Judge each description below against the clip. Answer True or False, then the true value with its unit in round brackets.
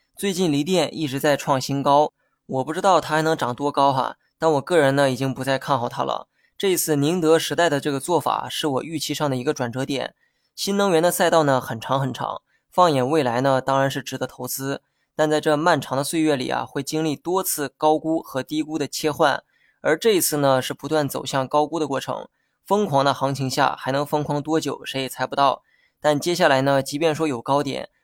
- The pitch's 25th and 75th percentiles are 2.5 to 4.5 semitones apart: True (2.8 semitones)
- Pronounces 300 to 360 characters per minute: True (310 characters per minute)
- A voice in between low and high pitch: True (145 Hz)